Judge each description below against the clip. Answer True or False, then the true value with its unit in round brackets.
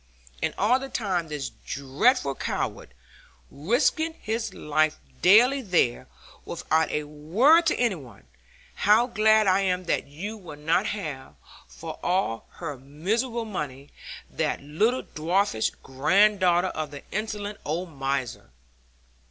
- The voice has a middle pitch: True (180 Hz)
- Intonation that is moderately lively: False (6.6 semitones)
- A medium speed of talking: False (125 wpm)